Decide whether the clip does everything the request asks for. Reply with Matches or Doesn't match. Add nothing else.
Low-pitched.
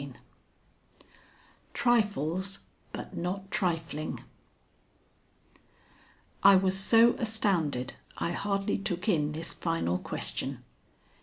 Doesn't match